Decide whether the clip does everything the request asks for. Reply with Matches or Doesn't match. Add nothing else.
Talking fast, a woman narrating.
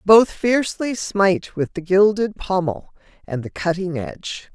Doesn't match